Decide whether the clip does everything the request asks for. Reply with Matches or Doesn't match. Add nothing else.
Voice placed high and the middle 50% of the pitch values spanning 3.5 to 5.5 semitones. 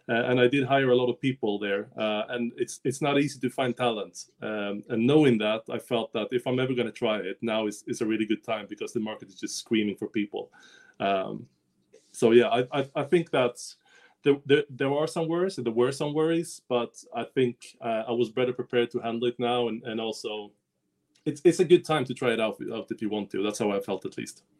Doesn't match